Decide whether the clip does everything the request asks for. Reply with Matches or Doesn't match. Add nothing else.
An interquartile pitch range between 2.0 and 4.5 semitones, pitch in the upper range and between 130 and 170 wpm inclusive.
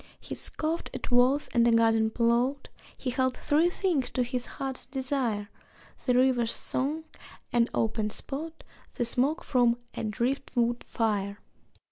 Matches